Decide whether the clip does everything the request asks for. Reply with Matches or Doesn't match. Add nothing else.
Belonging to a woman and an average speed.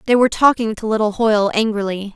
Matches